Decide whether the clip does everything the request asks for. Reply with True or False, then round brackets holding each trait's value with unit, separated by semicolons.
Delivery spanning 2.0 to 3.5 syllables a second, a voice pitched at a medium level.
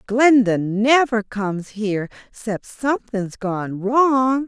False (3.4 syllables/s; 225 Hz)